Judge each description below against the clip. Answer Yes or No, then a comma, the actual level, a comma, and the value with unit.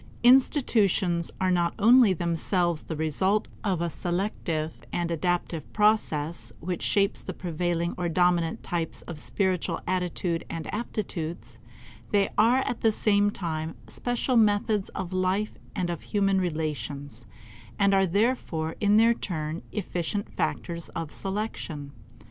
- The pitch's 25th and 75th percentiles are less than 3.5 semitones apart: No, average, 3.8 semitones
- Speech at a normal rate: No, slow, 130 wpm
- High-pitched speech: No, medium, 180 Hz